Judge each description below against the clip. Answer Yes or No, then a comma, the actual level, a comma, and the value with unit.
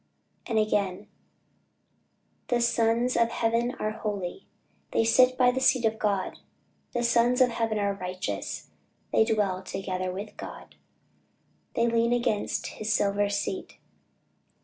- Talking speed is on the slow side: Yes, slow, 130 wpm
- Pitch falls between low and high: No, high, 220 Hz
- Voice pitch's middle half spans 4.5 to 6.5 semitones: No, average, 2.8 semitones